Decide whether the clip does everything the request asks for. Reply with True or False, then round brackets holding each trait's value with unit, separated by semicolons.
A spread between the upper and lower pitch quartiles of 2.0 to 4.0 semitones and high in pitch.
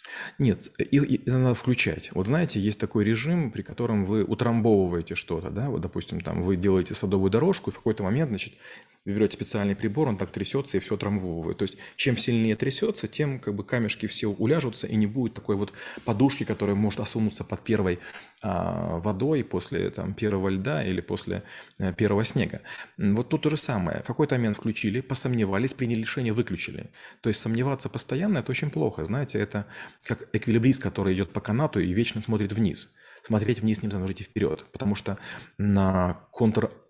False (3.6 semitones; 110 Hz)